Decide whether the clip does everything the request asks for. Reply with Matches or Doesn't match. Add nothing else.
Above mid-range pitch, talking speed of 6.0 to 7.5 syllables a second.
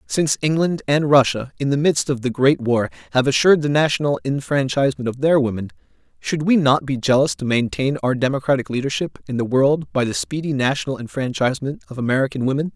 Doesn't match